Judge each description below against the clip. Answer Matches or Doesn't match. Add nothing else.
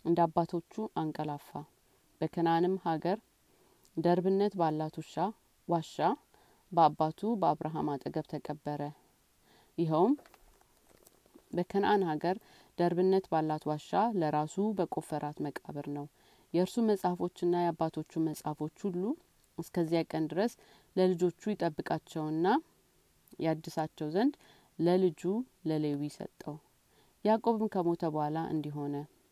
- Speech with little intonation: Doesn't match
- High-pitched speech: Doesn't match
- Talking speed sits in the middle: Doesn't match